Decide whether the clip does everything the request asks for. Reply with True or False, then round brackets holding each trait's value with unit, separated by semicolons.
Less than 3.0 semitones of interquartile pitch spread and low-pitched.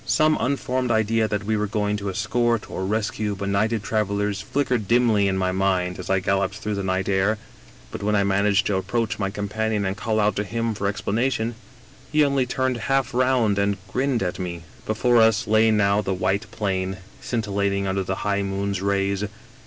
True (2.5 semitones; 105 Hz)